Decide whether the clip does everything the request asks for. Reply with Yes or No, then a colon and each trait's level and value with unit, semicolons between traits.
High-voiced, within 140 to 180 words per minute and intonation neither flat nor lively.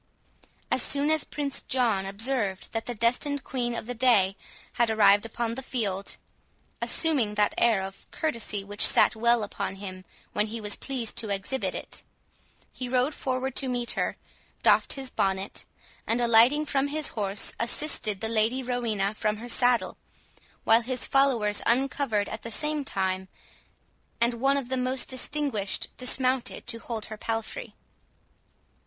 Yes: high, 235 Hz; average, 155 wpm; average, 3.8 semitones